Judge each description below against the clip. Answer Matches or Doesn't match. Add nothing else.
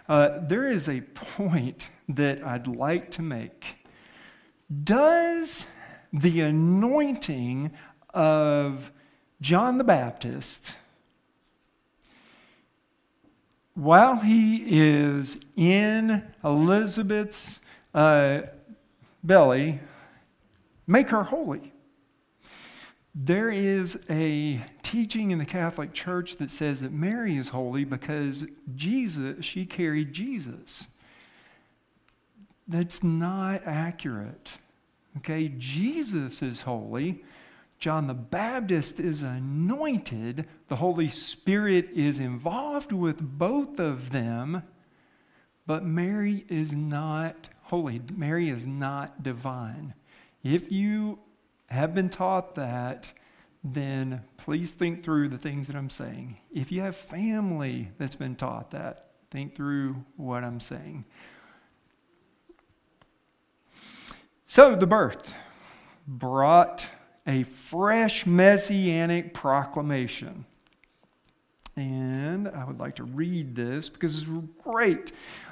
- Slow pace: Matches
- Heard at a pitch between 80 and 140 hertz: Doesn't match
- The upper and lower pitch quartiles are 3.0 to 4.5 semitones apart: Doesn't match